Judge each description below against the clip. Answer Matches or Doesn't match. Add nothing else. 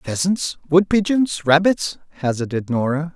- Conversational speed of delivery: Doesn't match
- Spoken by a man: Matches